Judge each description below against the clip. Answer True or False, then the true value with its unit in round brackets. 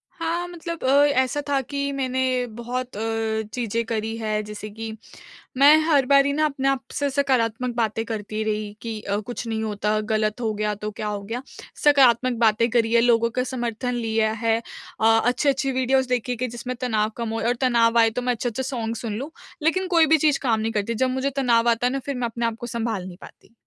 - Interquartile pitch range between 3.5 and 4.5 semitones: False (3.0 semitones)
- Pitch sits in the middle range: False (235 Hz)